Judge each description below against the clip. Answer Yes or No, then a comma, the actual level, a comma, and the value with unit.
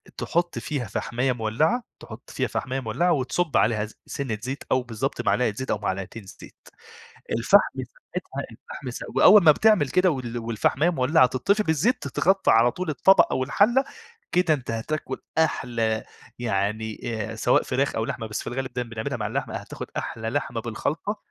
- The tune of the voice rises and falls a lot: Yes, wide, 6.1 semitones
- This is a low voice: Yes, low, 130 Hz